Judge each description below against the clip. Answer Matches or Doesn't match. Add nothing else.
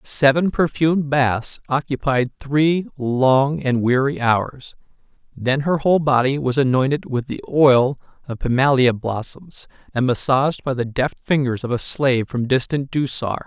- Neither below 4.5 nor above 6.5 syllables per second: Doesn't match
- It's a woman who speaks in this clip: Doesn't match